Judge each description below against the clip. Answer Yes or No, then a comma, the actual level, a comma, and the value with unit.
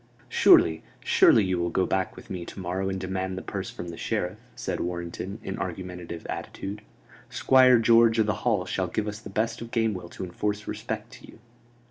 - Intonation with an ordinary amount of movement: Yes, average, 3.3 semitones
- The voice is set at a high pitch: No, very low, 95 Hz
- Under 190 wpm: No, average, 195 wpm